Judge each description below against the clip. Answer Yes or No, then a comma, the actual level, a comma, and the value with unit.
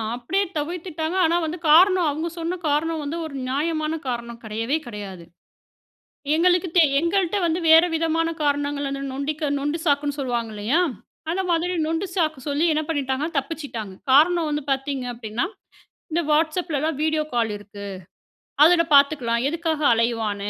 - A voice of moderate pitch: No, very high, 300 Hz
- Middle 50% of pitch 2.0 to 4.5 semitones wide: Yes, average, 3.9 semitones